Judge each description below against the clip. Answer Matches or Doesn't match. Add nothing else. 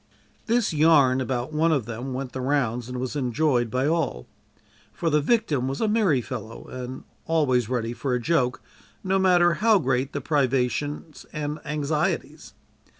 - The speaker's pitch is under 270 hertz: Matches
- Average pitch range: Matches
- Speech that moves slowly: Doesn't match